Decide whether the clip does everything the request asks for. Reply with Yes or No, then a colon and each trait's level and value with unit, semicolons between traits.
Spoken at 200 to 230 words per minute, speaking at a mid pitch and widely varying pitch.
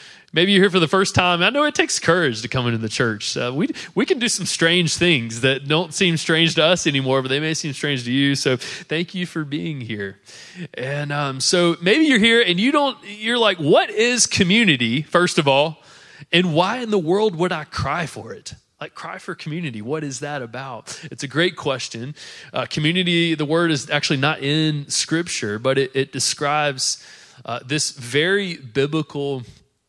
No: fast, 205 wpm; medium, 155 Hz; average, 4.7 semitones